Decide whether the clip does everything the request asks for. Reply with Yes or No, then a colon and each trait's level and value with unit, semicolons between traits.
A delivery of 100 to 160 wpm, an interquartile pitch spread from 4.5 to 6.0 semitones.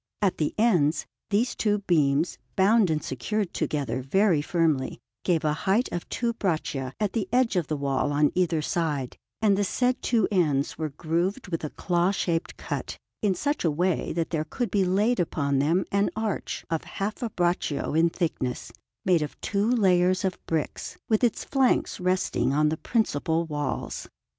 No: average, 175 wpm; average, 5.1 semitones